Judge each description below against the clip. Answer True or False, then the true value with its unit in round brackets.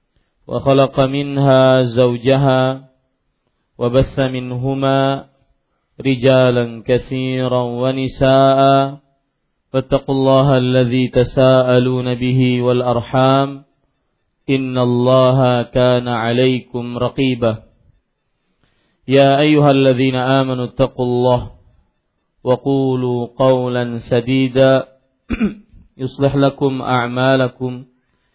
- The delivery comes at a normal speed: False (65 wpm)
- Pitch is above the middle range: False (130 Hz)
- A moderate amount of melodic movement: False (1.4 semitones)